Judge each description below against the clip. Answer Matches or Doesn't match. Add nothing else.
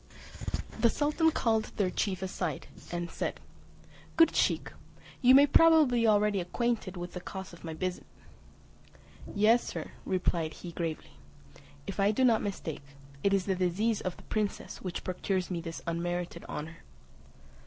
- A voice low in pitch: Doesn't match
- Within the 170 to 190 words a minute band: Doesn't match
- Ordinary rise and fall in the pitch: Matches